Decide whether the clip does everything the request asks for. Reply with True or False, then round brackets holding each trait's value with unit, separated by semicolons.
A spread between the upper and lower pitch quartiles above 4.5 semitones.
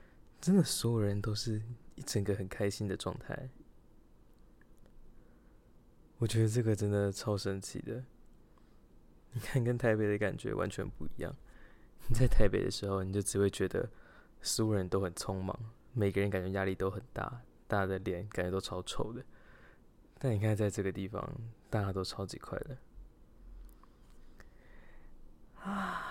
False (3.2 semitones)